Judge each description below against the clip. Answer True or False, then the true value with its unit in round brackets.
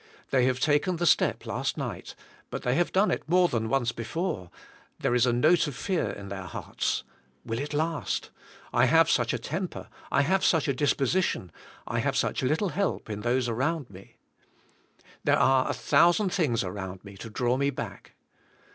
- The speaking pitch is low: True (130 Hz)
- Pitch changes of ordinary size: False (6.0 semitones)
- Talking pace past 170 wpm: True (185 wpm)